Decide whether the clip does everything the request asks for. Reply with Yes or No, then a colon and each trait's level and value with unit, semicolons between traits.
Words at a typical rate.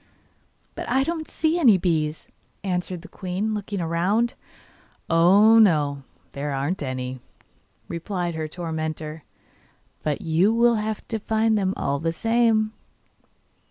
No: slow, 125 wpm